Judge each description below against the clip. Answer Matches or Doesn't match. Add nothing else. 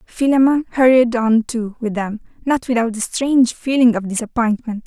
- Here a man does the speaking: Doesn't match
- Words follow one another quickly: Doesn't match